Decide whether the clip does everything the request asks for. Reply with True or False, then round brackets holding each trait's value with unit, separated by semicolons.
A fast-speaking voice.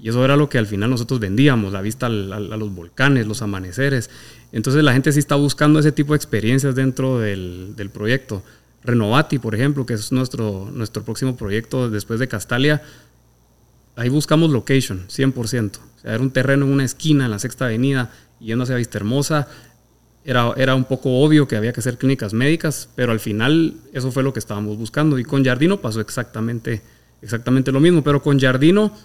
True (195 wpm)